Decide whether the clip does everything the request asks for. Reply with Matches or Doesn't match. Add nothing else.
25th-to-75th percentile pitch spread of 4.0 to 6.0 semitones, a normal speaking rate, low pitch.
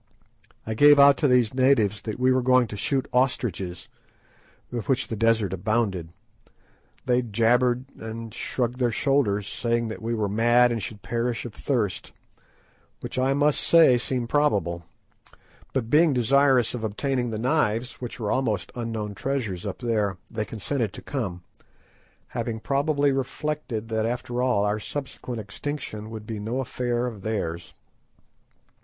Doesn't match